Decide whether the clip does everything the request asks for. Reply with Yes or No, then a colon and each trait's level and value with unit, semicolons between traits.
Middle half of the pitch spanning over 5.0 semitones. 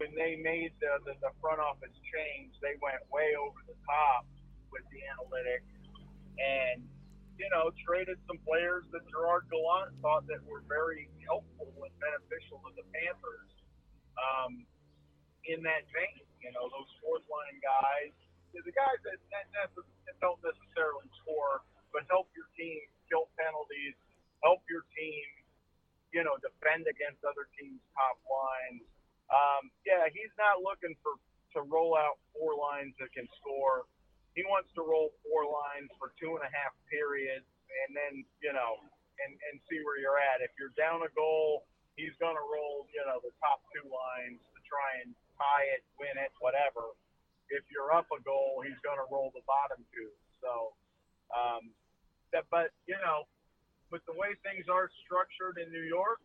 No: average, 4.1 semitones